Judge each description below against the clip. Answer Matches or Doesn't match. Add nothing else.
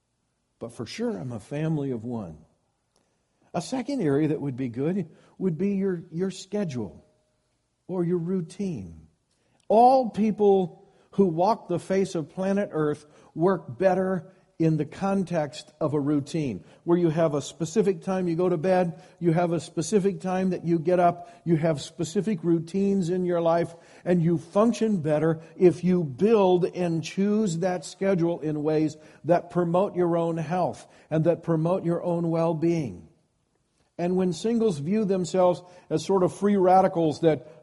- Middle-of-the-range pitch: Matches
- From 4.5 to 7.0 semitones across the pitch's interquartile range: Doesn't match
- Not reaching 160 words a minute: Doesn't match